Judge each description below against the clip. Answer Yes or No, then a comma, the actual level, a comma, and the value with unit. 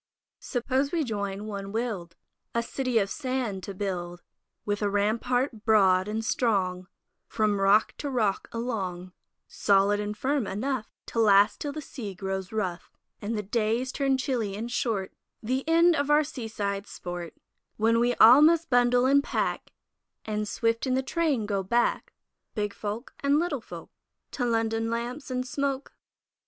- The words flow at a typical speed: Yes, average, 155 wpm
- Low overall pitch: No, high, 225 Hz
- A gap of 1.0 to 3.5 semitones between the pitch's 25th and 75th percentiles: No, average, 4.3 semitones